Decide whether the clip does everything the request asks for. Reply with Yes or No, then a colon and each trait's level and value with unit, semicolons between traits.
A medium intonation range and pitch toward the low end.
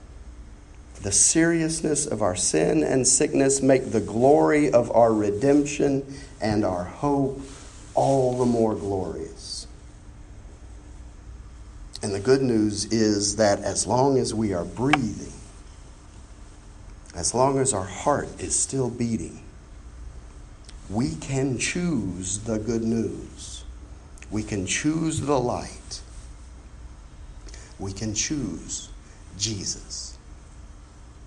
No: wide, 7.1 semitones; low, 100 Hz